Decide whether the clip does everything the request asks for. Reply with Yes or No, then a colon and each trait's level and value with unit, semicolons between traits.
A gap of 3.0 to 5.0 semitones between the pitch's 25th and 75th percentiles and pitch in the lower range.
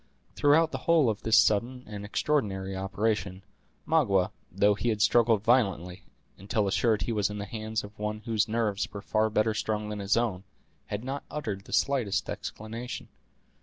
No: narrow, 2.6 semitones; low, 110 Hz